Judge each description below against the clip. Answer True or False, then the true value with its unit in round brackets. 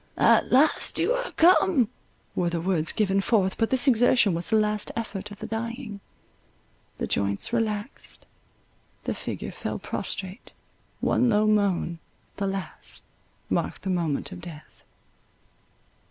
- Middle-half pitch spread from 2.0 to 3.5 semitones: False (4.0 semitones)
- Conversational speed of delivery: False (130 wpm)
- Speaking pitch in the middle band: False (205 Hz)